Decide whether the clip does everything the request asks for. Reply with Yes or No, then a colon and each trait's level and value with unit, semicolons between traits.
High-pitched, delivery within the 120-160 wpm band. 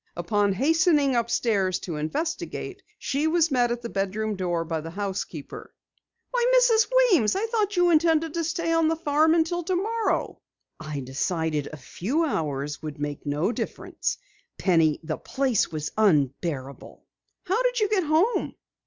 Yes: high, 235 Hz; average, 155 wpm